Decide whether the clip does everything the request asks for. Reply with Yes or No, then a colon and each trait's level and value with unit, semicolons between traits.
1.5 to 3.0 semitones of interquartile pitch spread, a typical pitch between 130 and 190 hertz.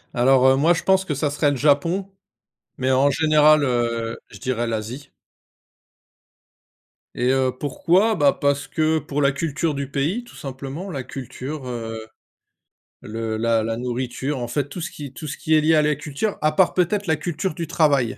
No: average, 3.7 semitones; medium, 140 Hz